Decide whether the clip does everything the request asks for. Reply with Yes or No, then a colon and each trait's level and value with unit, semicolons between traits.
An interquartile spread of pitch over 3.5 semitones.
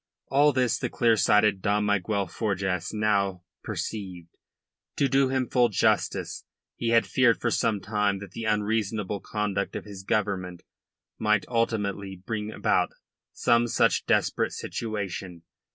No: average, 2.7 semitones